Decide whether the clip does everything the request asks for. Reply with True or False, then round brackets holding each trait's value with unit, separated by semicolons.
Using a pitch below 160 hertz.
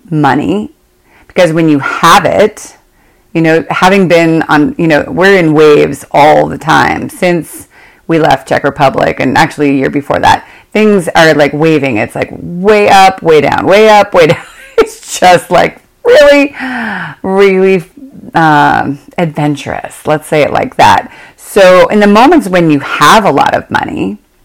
False (175 Hz)